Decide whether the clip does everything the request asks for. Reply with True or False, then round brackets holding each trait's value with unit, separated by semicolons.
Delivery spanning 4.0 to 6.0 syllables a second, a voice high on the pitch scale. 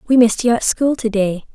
False (6.2 syllables/s; 230 Hz)